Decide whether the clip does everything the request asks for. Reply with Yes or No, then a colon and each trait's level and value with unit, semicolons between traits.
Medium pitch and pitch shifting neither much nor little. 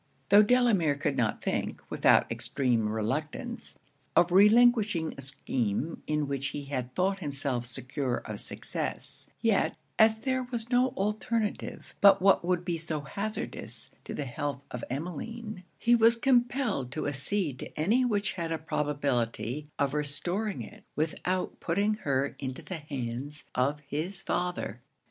No: medium, 160 Hz; wide, 7.2 semitones